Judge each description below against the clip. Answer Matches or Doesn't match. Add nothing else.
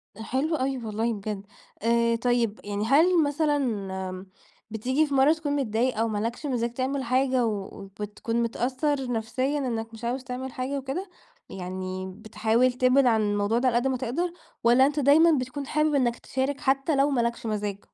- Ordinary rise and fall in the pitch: Matches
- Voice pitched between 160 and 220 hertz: Doesn't match